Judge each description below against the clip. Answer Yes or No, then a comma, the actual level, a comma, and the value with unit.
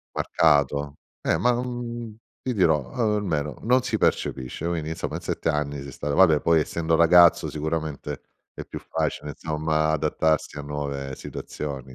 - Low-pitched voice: Yes, very low, 80 Hz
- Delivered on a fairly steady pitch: No, average, 3.1 semitones